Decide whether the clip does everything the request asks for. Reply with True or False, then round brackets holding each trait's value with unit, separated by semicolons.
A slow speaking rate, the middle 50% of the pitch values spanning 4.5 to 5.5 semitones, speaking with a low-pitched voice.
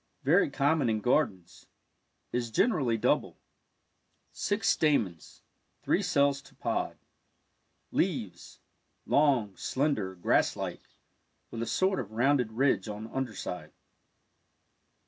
True (120 wpm; 5.2 semitones; 125 Hz)